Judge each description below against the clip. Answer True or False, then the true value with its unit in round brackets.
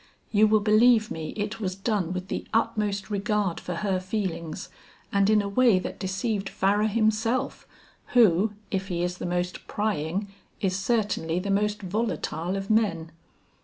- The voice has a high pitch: True (200 Hz)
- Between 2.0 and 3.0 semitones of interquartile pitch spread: True (2.7 semitones)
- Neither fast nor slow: True (160 wpm)